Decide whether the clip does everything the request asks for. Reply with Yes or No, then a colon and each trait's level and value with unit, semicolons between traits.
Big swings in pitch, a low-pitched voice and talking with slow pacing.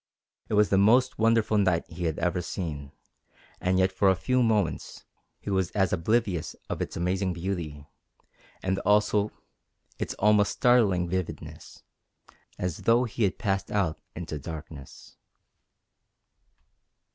No: average, 3.4 semitones; very low, 95 Hz; slow, 125 wpm